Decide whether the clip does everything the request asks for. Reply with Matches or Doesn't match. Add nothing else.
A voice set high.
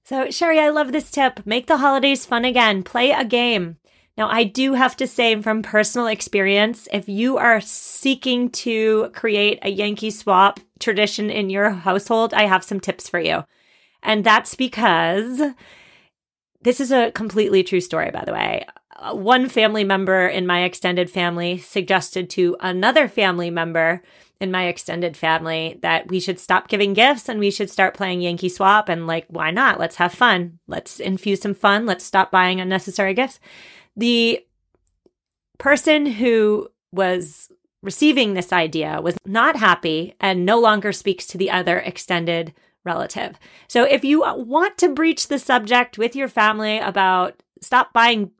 Matches